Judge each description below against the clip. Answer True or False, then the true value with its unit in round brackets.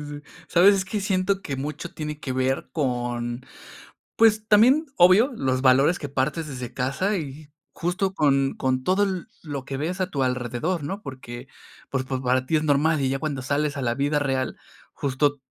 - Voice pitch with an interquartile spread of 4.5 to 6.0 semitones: True (5.4 semitones)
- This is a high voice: False (145 Hz)